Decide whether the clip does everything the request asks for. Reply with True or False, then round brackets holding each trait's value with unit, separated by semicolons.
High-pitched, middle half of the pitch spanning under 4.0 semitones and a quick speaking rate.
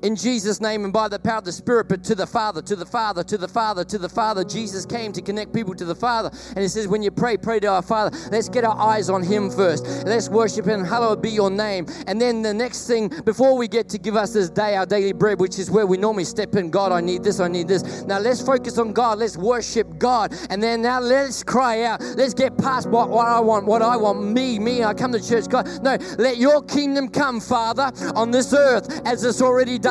True (220 Hz; 3.0 semitones; 260 wpm)